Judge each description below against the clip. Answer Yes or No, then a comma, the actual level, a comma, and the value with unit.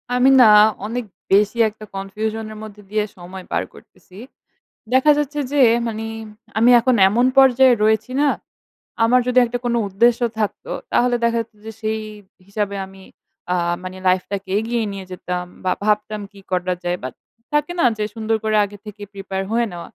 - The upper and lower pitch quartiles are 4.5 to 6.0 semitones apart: No, average, 3.5 semitones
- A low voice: No, high, 215 Hz